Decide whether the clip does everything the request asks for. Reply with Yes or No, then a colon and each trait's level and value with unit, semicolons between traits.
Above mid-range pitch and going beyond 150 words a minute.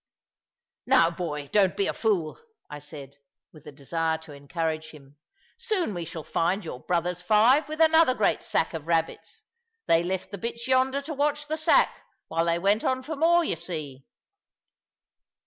No: medium, 175 Hz; average, 170 wpm